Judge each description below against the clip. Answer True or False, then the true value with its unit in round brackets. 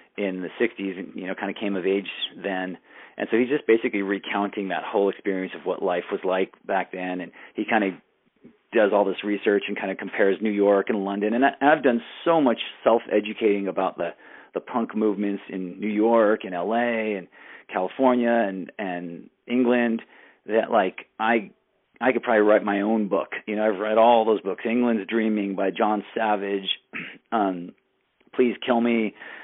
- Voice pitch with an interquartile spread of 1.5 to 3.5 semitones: True (2.6 semitones)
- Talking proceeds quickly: False (190 wpm)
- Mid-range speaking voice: False (105 Hz)